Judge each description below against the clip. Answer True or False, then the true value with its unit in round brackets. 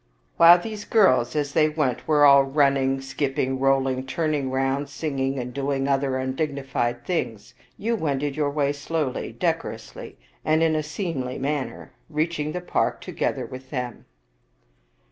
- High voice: False (140 Hz)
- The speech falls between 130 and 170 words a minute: True (160 wpm)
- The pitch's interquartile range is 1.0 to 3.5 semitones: True (2.6 semitones)